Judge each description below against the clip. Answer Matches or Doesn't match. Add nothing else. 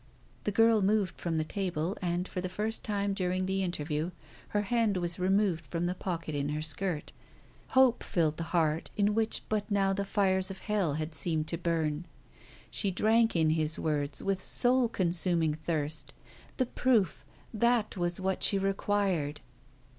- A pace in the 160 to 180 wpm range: Matches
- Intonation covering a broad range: Doesn't match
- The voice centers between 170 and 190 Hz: Matches